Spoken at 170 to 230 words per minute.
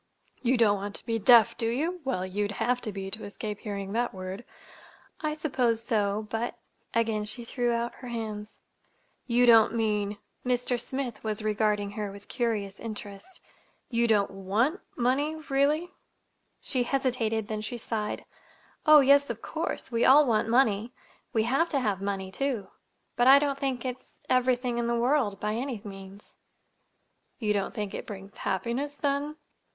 No: average, 160 wpm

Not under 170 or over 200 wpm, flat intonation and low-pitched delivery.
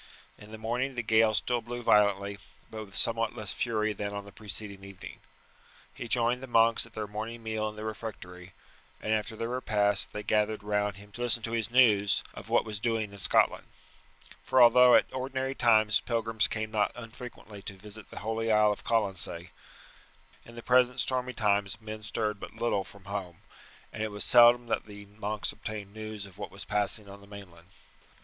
Yes: average, 195 wpm; narrow, 2.2 semitones; low, 110 Hz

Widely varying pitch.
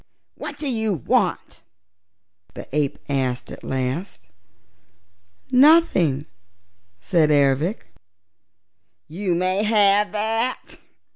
Yes: wide, 7.4 semitones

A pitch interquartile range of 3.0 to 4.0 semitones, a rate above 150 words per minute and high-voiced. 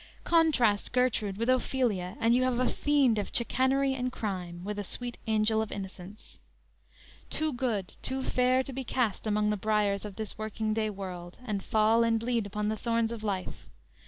Yes: average, 3.4 semitones; average, 185 wpm; high, 220 Hz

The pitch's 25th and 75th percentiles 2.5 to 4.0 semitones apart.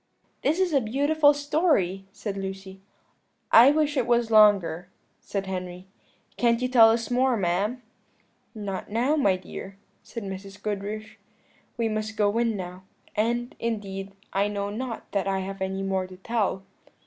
Yes: average, 3.7 semitones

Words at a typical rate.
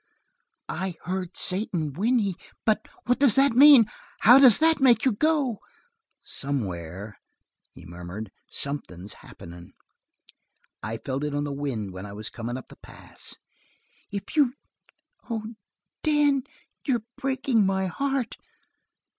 No: slow, 130 wpm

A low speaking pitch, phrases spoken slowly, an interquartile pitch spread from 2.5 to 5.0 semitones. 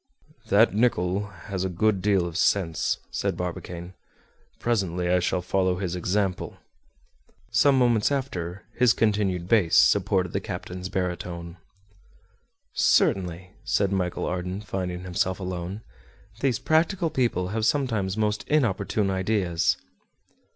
Yes: very low, 95 Hz; slow, 120 wpm; average, 3.2 semitones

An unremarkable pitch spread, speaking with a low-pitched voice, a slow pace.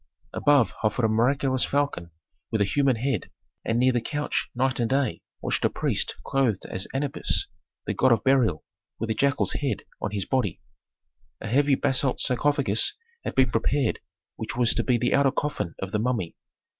No: average, 3.6 semitones; low, 125 Hz; average, 180 wpm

